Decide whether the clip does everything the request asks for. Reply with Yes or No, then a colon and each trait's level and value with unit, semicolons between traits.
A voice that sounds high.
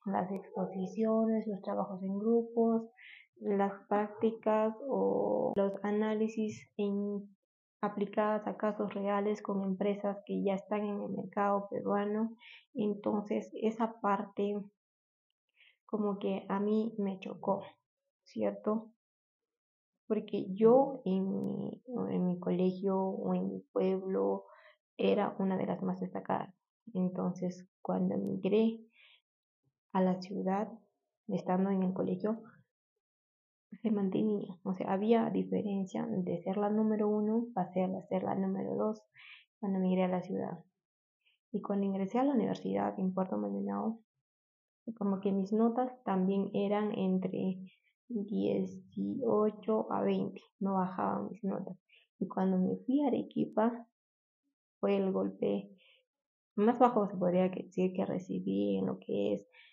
Yes: high, 200 Hz